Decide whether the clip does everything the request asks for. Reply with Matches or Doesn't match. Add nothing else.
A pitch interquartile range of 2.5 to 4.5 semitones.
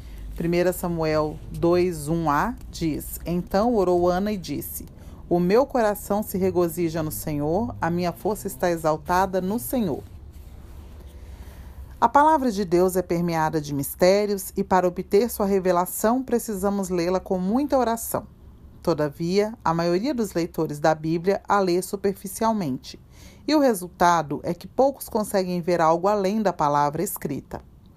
Matches